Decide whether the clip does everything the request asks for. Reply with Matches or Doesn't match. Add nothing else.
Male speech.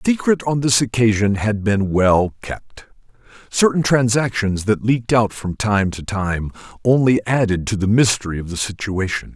Matches